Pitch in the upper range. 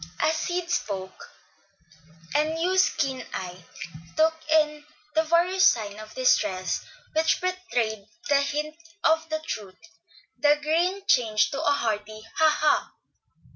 Yes: very high, 300 Hz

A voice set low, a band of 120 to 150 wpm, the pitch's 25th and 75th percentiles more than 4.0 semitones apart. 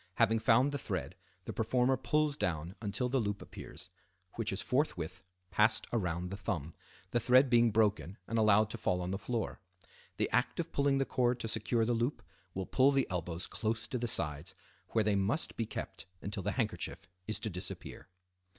No: low, 110 Hz; average, 190 wpm; average, 4.4 semitones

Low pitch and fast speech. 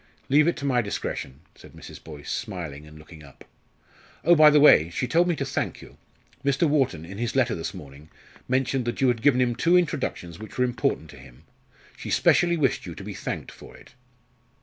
Yes: low, 120 Hz; fast, 210 wpm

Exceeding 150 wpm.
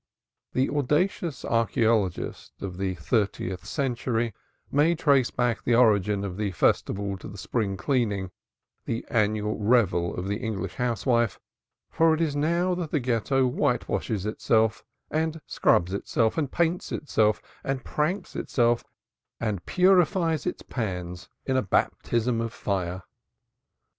No: slow, 135 wpm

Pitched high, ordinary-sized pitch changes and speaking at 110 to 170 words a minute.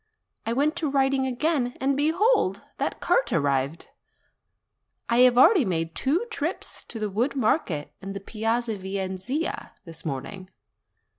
No: high, 235 Hz; wide, 6.7 semitones; average, 140 wpm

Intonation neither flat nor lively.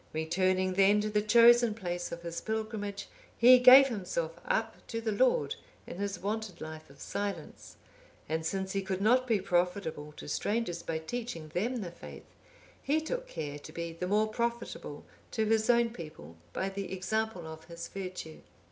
Yes: average, 4.7 semitones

